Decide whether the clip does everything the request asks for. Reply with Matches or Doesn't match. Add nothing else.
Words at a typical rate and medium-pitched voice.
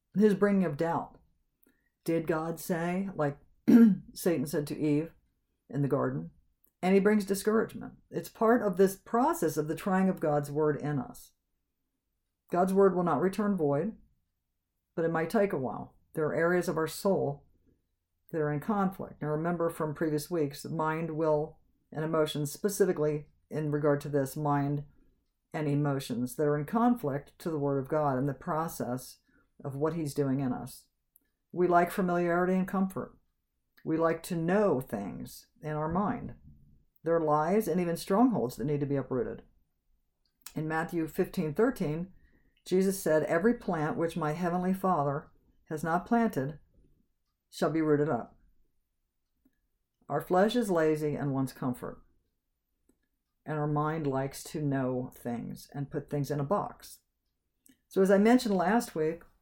Matches